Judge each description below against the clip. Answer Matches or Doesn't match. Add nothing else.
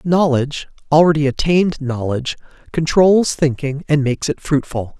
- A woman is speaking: Doesn't match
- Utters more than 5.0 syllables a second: Matches